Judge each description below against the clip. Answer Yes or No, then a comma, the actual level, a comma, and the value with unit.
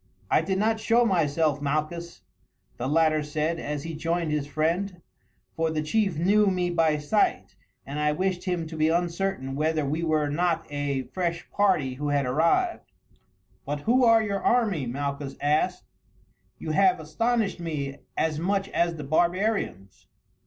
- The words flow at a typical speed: Yes, average, 160 wpm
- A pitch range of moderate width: Yes, average, 4.2 semitones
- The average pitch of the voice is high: No, medium, 160 Hz